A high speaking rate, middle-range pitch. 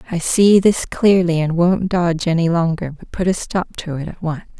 Yes: fast, 220 wpm; medium, 175 Hz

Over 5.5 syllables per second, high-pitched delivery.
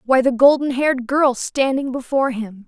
No: 5.1 syllables/s; very high, 260 Hz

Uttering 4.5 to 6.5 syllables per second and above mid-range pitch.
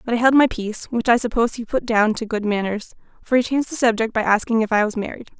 No: 6.7 syllables/s; high, 230 Hz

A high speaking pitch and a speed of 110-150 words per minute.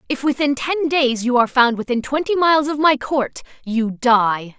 No: very high, 265 Hz; average, 195 wpm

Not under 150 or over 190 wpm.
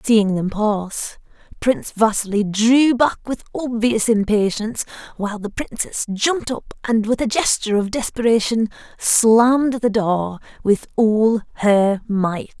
No: slow, 135 wpm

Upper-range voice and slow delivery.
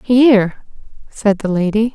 Yes: high, 215 Hz; slow, 125 wpm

